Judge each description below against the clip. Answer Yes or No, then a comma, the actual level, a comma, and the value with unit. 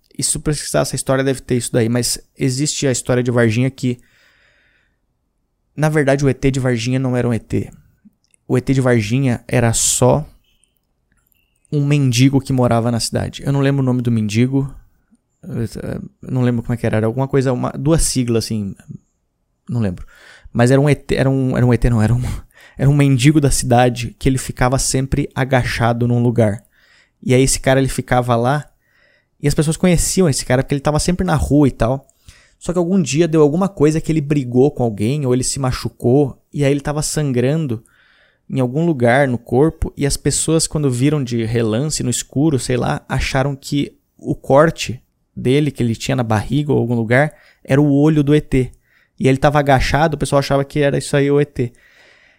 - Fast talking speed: Yes, fast, 195 wpm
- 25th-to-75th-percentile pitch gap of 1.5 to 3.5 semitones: Yes, average, 3.1 semitones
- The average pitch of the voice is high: No, low, 130 Hz